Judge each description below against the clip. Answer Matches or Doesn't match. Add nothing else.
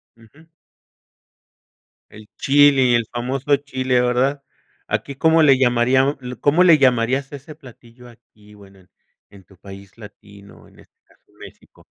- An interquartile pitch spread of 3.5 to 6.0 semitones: Matches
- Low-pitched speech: Matches